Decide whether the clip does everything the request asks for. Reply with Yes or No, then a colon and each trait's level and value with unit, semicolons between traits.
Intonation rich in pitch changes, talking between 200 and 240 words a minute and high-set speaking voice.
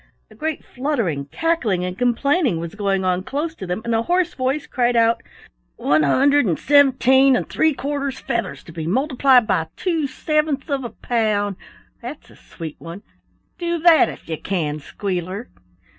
No: wide, 7.5 semitones; average, 170 wpm; high, 245 Hz